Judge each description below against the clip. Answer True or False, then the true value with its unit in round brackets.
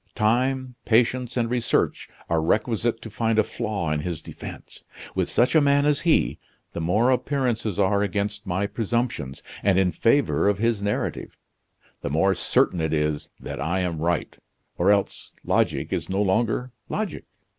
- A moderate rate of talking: True (165 wpm)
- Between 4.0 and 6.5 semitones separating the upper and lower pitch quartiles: True (5.2 semitones)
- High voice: False (105 Hz)